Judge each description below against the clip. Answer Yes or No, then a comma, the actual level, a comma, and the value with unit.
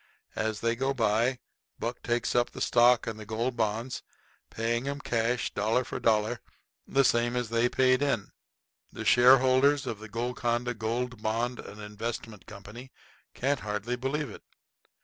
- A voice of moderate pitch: No, low, 120 Hz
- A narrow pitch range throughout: Yes, narrow, 2.2 semitones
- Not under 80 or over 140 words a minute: No, average, 155 wpm